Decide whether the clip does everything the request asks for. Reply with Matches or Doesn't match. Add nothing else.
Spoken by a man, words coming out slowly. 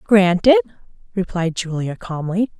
Doesn't match